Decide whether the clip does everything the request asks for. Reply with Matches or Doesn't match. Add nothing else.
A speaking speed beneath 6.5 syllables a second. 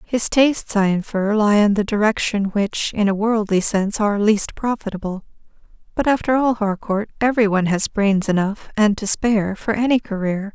Matches